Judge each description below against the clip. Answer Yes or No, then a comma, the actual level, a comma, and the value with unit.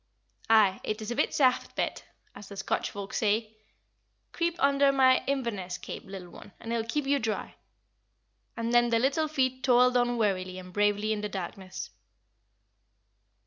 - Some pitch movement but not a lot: Yes, average, 4.2 semitones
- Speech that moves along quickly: No, average, 170 wpm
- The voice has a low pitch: No, high, 225 Hz